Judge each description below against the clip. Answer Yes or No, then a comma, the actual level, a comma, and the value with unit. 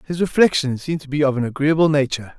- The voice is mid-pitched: Yes, medium, 145 Hz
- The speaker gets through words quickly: Yes, fast, 225 wpm